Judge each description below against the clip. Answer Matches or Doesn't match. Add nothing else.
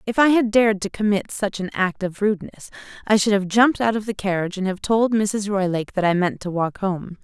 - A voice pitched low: Doesn't match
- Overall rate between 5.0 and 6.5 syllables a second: Matches